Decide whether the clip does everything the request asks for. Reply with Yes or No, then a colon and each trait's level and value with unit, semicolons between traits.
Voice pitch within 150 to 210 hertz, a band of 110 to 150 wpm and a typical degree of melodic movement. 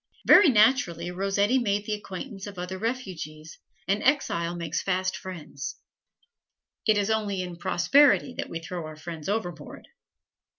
Yes: high, 190 Hz; average, 140 wpm; average, 4.0 semitones